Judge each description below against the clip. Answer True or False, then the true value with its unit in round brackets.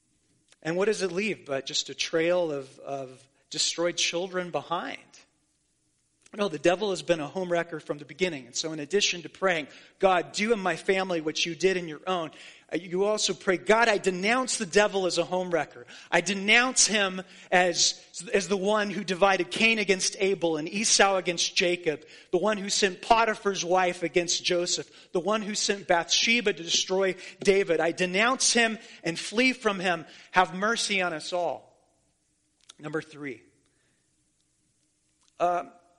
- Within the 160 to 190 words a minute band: True (170 wpm)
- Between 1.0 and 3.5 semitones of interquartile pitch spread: True (3.2 semitones)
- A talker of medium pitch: True (180 Hz)